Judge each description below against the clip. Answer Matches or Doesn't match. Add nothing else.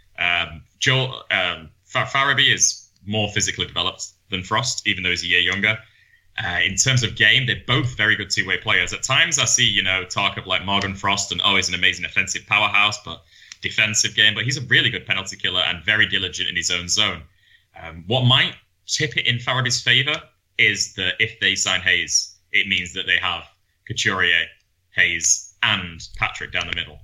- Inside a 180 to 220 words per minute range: Matches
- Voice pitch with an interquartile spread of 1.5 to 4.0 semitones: Matches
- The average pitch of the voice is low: Matches